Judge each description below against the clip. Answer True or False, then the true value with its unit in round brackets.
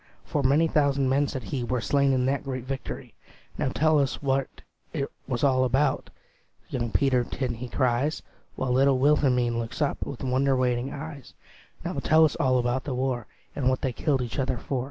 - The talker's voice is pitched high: False (130 Hz)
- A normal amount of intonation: False (1.9 semitones)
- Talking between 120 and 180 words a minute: False (190 wpm)